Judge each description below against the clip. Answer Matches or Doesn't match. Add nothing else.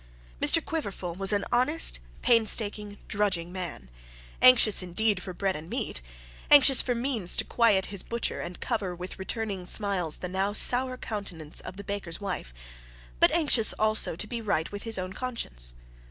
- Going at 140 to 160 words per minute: Doesn't match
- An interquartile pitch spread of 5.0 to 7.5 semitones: Doesn't match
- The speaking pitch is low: Doesn't match